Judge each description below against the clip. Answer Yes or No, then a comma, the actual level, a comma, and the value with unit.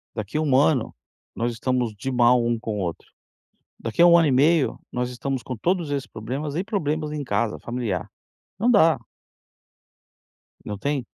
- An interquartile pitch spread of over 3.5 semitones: Yes, average, 4.6 semitones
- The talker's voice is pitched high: No, low, 130 Hz